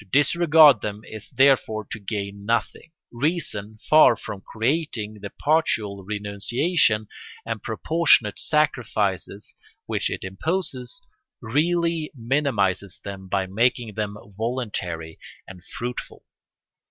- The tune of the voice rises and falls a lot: Yes, wide, 6.5 semitones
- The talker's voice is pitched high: No, low, 110 Hz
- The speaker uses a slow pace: Yes, slow, 105 wpm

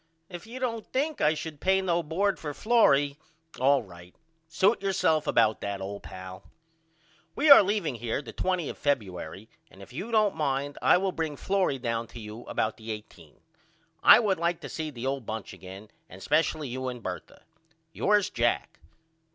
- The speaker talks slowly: No, average, 180 wpm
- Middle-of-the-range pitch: Yes, medium, 145 Hz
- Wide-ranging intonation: Yes, wide, 9.0 semitones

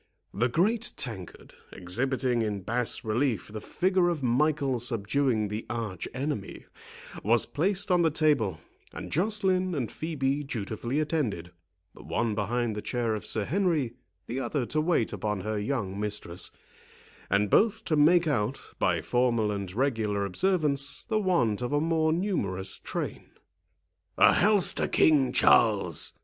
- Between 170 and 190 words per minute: No, average, 145 wpm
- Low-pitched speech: Yes, low, 125 Hz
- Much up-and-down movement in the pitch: Yes, wide, 6.9 semitones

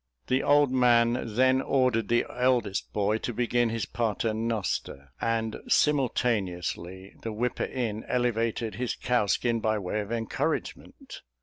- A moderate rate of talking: No, slow, 130 wpm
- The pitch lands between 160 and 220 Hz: No, low, 115 Hz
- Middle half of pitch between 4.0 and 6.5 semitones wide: No, narrow, 2.4 semitones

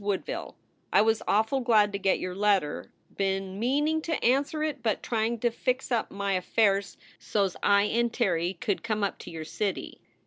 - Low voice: No, high, 210 Hz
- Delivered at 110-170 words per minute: No, average, 180 wpm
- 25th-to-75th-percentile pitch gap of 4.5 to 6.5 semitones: No, average, 3.5 semitones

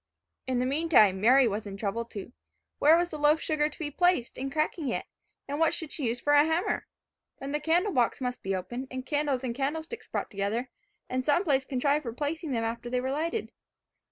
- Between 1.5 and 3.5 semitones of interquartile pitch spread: No, average, 4.3 semitones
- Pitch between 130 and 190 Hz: No, very high, 275 Hz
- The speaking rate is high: Yes, fast, 220 wpm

